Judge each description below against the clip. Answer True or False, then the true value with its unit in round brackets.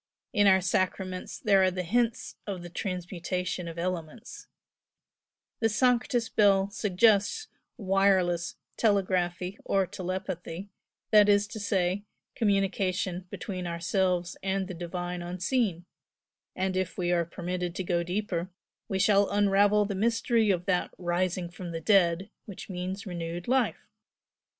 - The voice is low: False (185 Hz)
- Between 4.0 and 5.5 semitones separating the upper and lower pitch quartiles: False (2.4 semitones)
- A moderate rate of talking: False (130 wpm)